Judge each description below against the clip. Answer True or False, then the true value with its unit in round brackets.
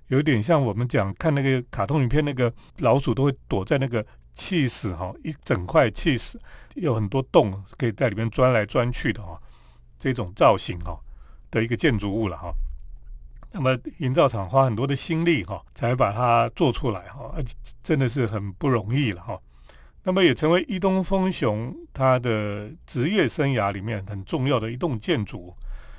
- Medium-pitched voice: False (115 Hz)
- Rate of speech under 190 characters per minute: False (260 characters per minute)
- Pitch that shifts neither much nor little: False (6.0 semitones)